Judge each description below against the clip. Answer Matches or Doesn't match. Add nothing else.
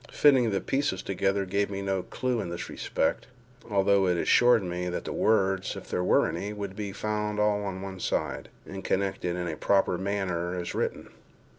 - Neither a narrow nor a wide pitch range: Doesn't match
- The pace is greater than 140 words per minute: Matches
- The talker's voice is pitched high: Doesn't match